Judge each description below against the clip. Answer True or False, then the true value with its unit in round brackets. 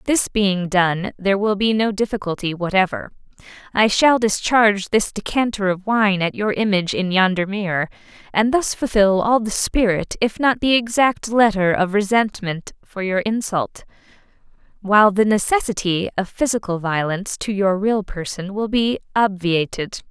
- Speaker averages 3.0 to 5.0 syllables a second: True (4.8 syllables/s)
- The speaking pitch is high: True (205 Hz)